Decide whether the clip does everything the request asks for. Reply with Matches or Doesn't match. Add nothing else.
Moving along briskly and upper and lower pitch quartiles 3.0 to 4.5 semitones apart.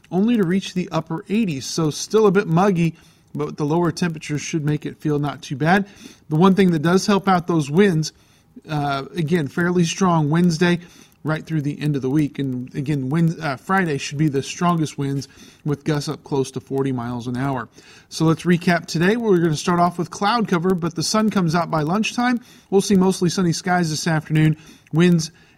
Matches